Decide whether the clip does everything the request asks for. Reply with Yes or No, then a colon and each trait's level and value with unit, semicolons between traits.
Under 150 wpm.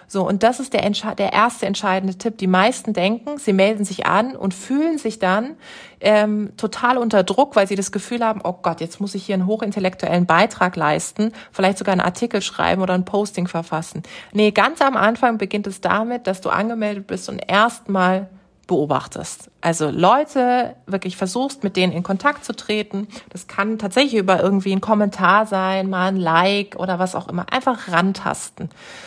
No: average, 185 wpm